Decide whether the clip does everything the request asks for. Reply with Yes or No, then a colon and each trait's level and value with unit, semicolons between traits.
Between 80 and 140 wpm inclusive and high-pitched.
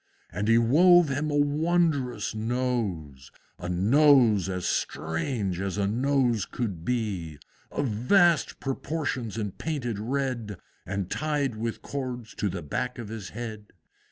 No: slow, 135 wpm; low, 115 Hz